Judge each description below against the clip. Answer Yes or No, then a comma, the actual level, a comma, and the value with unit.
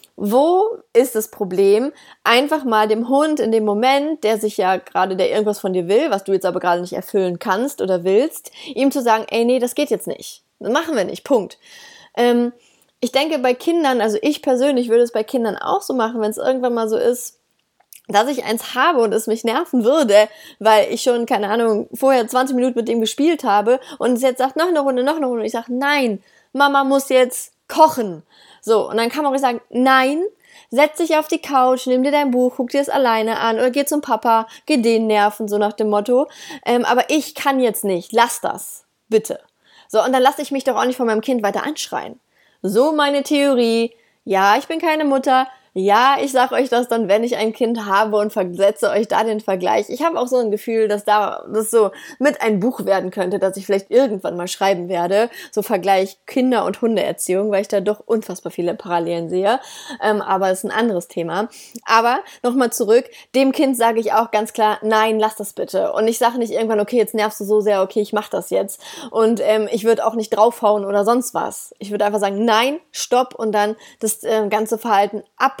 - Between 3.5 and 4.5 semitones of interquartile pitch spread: Yes, average, 4.1 semitones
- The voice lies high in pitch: Yes, high, 230 Hz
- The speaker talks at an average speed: No, fast, 220 wpm